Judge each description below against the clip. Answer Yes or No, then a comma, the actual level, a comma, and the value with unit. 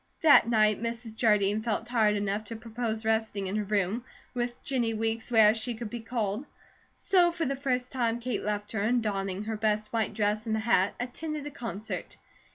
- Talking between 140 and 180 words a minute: No, average, 195 wpm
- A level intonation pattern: Yes, narrow, 2.3 semitones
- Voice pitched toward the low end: No, high, 225 Hz